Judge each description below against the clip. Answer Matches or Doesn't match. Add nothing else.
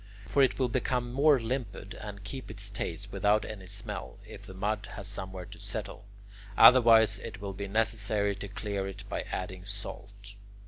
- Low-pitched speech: Matches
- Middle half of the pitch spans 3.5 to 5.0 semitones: Doesn't match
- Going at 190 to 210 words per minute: Doesn't match